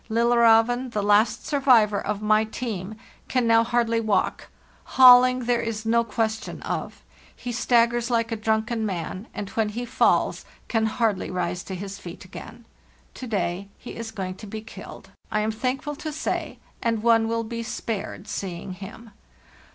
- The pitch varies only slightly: Yes, narrow, 2.2 semitones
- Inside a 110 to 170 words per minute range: Yes, average, 165 wpm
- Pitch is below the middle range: No, high, 225 Hz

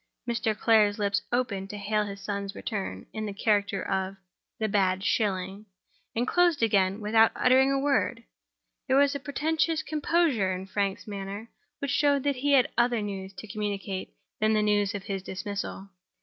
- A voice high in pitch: Yes, high, 210 Hz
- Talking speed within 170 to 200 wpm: Yes, average, 175 wpm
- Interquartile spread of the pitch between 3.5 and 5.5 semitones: Yes, average, 4.1 semitones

